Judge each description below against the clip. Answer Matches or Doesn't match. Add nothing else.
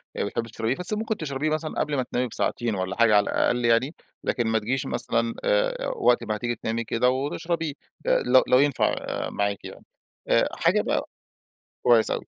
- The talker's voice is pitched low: Matches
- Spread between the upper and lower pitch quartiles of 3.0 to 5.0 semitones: Matches